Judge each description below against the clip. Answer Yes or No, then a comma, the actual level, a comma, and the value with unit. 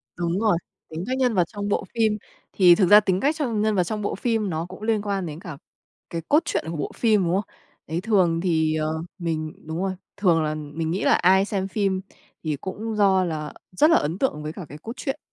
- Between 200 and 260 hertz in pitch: No, high, 190 Hz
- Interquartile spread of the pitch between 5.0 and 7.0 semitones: No, average, 4.4 semitones